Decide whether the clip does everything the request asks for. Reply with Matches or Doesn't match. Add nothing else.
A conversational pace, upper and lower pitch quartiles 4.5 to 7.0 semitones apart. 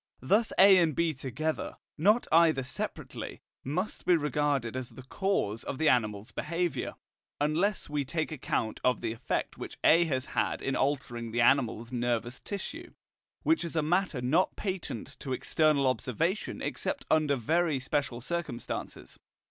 Matches